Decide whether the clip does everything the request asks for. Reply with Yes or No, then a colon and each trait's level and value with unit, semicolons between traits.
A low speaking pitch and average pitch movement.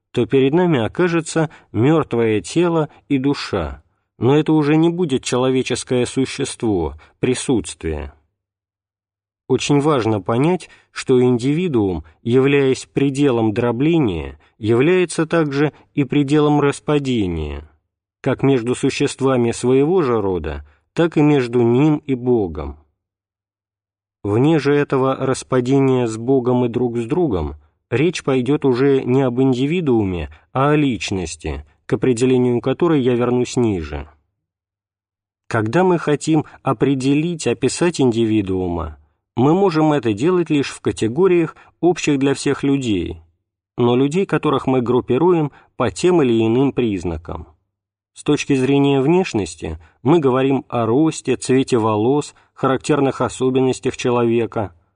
No: low, 125 Hz; wide, 6.2 semitones